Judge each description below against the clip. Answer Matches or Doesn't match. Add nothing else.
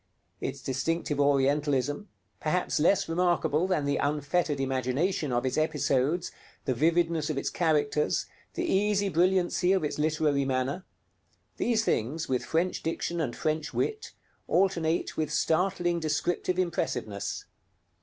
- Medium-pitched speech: Matches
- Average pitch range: Matches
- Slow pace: Matches